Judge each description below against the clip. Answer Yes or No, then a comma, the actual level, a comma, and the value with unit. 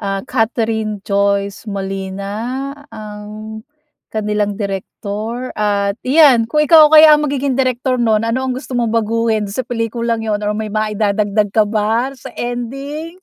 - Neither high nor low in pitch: No, high, 220 Hz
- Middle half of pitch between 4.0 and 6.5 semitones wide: No, average, 3.3 semitones